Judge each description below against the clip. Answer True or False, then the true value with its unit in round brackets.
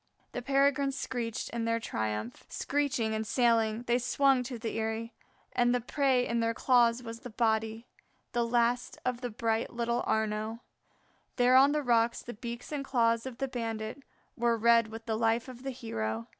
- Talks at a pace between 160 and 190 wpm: True (180 wpm)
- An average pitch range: False (1.9 semitones)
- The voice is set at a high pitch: True (235 Hz)